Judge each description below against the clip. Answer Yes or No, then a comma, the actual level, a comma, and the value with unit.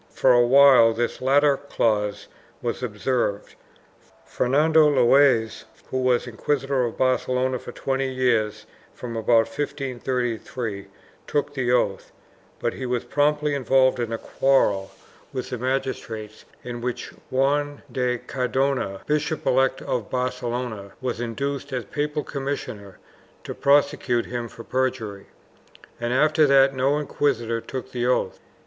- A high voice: No, low, 130 Hz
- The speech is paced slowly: Yes, slow, 130 wpm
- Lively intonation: No, average, 2.8 semitones